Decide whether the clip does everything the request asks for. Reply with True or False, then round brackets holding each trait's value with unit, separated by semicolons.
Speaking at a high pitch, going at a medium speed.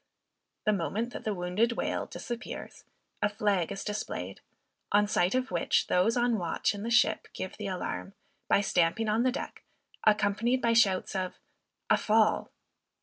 True (210 Hz; 160 wpm)